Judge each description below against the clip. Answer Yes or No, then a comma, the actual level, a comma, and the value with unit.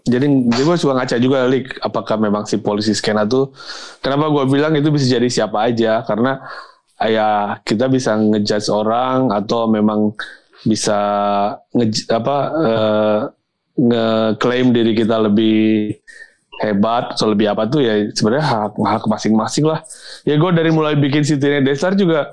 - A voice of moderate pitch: No, low, 115 Hz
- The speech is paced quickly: Yes, fast, 155 wpm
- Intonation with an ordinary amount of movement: Yes, average, 4.2 semitones